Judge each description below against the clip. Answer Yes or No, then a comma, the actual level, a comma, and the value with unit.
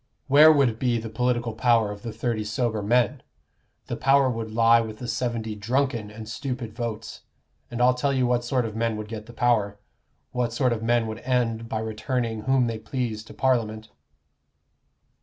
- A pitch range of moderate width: No, narrow, 2.1 semitones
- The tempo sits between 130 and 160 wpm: No, average, 185 wpm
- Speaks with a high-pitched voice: No, low, 115 Hz